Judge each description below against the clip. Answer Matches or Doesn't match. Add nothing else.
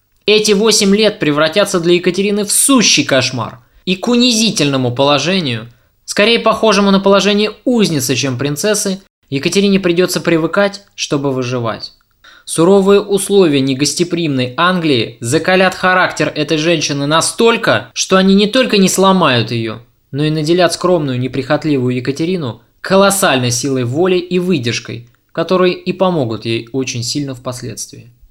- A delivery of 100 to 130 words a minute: Matches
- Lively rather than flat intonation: Matches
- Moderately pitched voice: Matches